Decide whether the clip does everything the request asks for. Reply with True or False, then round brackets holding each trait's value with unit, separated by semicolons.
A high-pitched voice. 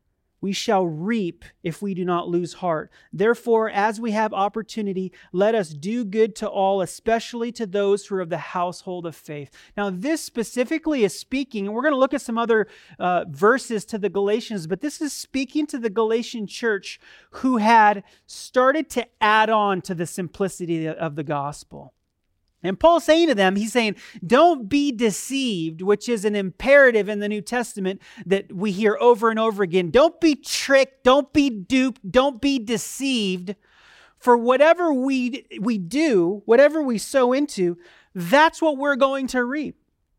True (220 Hz)